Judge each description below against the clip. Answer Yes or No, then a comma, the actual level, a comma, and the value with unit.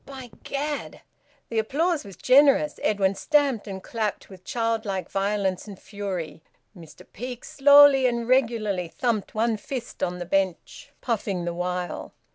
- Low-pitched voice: No, high, 215 Hz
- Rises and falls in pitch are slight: No, average, 5.1 semitones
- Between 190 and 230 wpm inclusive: No, average, 140 wpm